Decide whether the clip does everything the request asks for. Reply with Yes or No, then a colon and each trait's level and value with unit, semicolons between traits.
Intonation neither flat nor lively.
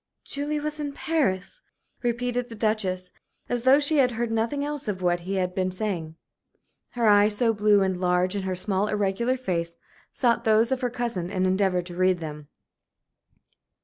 Yes: average, 5.0 semitones